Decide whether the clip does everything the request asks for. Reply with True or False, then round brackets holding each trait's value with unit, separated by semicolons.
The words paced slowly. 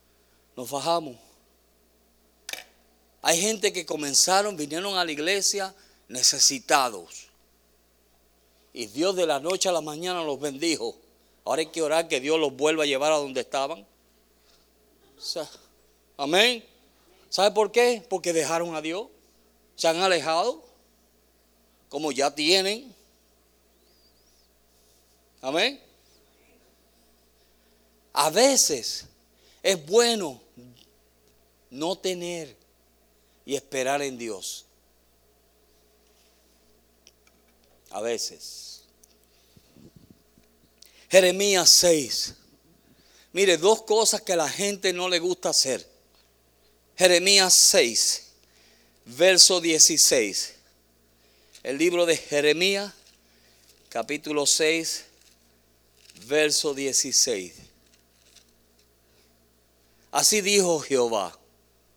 True (90 wpm)